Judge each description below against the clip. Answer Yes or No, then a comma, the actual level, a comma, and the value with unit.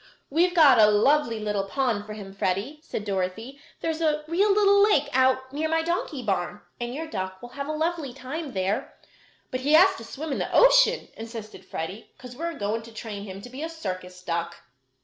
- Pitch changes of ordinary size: No, wide, 7.3 semitones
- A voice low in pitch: No, very high, 255 Hz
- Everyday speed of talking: No, fast, 210 wpm